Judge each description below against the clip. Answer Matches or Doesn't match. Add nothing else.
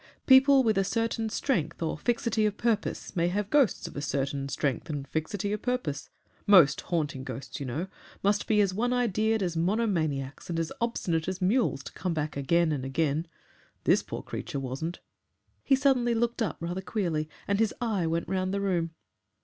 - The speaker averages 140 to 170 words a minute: Doesn't match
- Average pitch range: Doesn't match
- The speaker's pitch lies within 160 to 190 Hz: Matches